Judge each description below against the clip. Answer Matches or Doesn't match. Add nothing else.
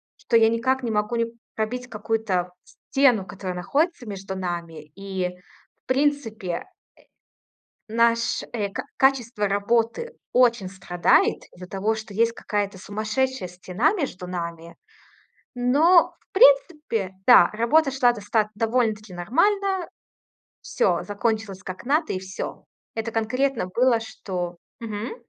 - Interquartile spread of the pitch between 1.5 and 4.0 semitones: Doesn't match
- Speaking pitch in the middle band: Doesn't match